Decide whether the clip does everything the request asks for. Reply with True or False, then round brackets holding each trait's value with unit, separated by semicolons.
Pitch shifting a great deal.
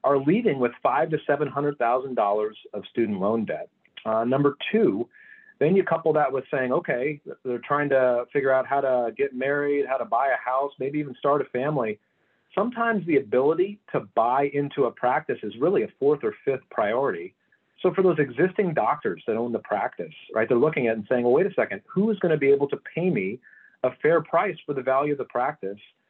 True (7.3 semitones)